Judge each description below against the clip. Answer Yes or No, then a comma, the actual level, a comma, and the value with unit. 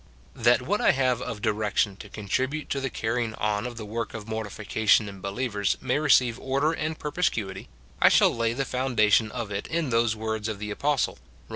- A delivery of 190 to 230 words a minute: Yes, average, 195 wpm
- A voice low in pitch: Yes, low, 115 Hz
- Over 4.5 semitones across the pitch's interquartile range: No, average, 3.7 semitones